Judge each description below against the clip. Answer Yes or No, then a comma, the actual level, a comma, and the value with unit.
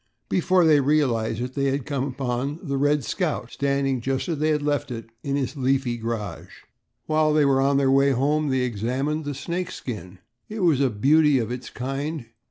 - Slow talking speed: No, average, 195 wpm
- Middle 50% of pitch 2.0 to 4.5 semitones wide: Yes, average, 2.9 semitones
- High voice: No, medium, 140 Hz